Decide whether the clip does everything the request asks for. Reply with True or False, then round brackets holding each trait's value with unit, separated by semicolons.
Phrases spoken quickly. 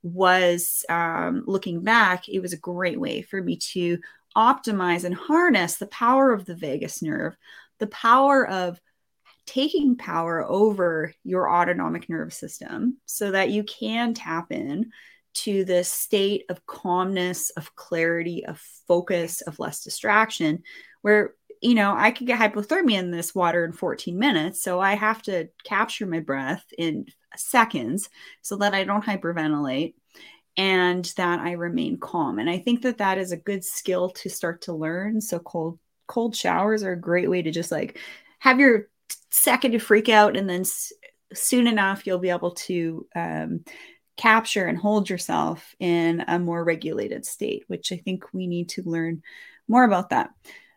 False (165 wpm)